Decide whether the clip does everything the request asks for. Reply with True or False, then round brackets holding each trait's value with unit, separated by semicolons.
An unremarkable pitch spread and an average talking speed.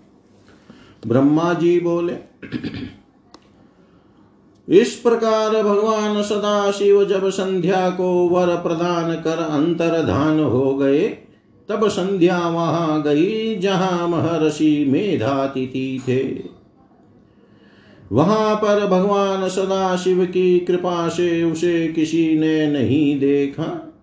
False (3.9 semitones; 90 wpm)